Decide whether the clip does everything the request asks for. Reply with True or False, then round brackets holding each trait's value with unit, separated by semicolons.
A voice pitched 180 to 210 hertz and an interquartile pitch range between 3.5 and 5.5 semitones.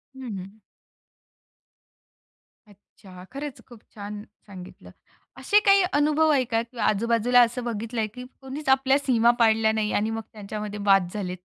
False (225 Hz; 3.9 semitones)